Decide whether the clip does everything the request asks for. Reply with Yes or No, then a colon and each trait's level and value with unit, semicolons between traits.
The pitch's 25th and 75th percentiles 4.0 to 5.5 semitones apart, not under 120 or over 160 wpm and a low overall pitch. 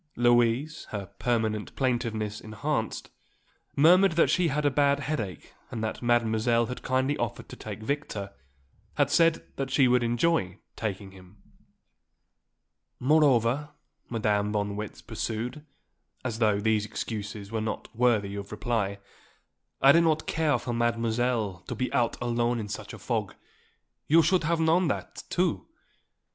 Yes: average, 4.8 semitones; average, 145 wpm; low, 120 Hz